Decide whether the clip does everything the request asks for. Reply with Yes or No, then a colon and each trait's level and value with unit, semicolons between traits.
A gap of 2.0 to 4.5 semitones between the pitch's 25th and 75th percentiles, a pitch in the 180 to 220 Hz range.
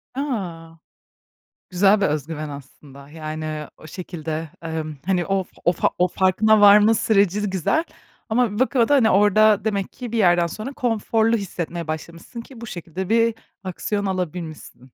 No: average, 5.0 semitones; high, 190 Hz